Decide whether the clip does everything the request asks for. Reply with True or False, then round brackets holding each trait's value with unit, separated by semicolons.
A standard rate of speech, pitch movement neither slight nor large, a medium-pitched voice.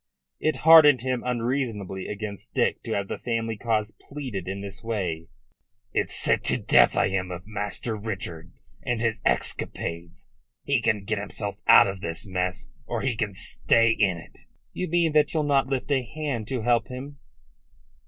False (175 wpm; 4.8 semitones; 110 Hz)